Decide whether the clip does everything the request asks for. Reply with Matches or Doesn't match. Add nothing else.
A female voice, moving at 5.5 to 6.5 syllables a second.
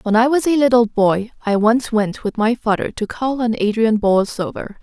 Doesn't match